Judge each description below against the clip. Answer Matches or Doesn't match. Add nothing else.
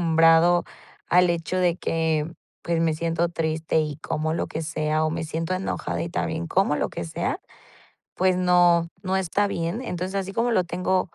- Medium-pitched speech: Matches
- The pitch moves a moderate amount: Doesn't match